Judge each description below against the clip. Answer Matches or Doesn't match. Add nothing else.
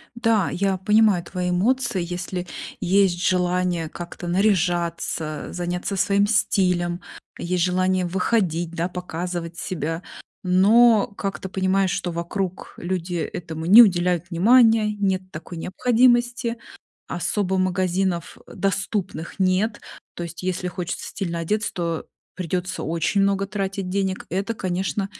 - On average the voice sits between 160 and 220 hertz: Matches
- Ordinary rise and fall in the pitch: Doesn't match